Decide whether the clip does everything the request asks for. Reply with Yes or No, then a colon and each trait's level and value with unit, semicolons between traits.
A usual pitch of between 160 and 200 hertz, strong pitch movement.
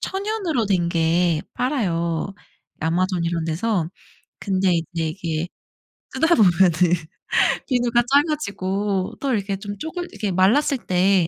Yes: high, 190 Hz; wide, 6.0 semitones